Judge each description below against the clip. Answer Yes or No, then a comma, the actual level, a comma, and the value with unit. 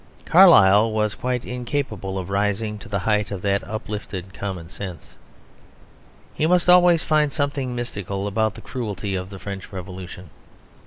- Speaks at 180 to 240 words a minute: No, average, 150 wpm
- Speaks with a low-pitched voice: Yes, low, 105 Hz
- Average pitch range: Yes, average, 4.3 semitones